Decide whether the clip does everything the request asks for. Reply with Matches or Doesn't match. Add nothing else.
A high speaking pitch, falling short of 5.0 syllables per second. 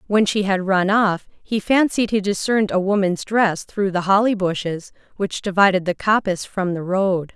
Matches